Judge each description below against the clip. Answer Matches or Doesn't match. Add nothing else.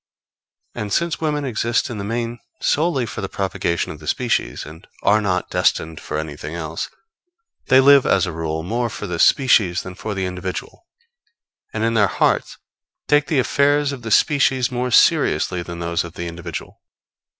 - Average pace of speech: Matches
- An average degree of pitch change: Doesn't match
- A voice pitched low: Matches